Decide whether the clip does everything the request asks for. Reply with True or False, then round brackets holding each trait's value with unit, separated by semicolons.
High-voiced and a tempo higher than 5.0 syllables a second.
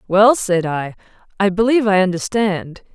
False (195 Hz; 4.9 syllables/s)